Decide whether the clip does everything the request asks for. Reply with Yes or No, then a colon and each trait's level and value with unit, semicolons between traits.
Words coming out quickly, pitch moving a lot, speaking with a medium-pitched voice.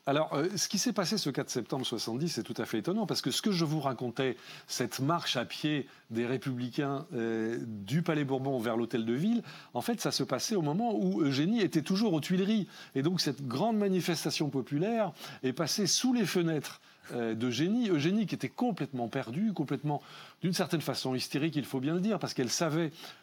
No: average, 205 wpm; wide, 5.9 semitones; medium, 150 Hz